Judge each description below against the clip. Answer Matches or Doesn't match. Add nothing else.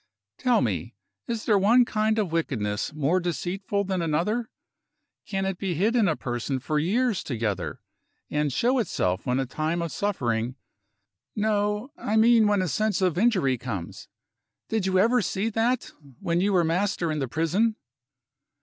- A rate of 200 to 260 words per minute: Doesn't match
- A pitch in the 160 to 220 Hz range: Matches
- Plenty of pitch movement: Matches